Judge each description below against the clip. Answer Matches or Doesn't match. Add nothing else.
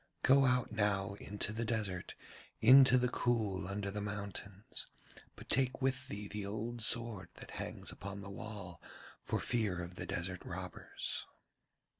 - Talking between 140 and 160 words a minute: Matches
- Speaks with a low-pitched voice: Matches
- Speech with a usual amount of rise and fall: Matches